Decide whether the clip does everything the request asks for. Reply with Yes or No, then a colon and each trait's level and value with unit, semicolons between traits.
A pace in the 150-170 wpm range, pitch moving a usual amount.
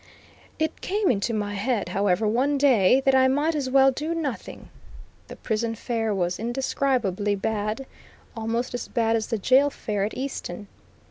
Yes: average, 160 wpm; average, 4.3 semitones